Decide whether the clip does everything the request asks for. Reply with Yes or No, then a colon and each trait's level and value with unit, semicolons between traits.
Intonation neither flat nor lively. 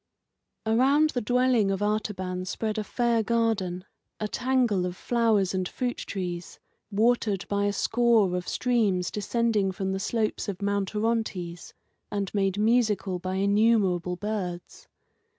Yes: average, 3.5 semitones